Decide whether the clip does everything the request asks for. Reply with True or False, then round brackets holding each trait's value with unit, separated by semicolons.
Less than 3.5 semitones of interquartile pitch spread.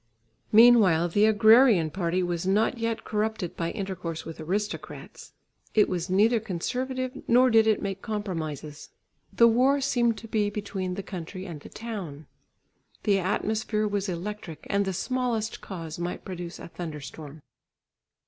False (4.3 semitones)